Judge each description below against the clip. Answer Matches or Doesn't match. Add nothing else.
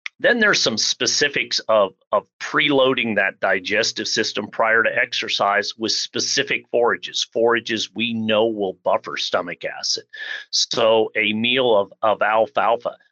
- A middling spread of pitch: Matches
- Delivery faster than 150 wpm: Doesn't match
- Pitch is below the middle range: Matches